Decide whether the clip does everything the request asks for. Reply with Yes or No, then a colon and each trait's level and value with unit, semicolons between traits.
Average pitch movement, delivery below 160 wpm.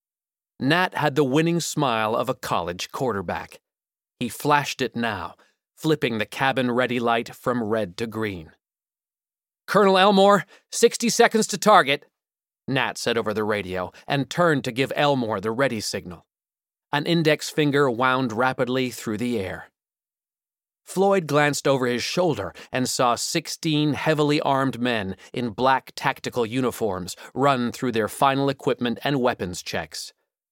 Yes: average, 4.2 semitones; average, 140 wpm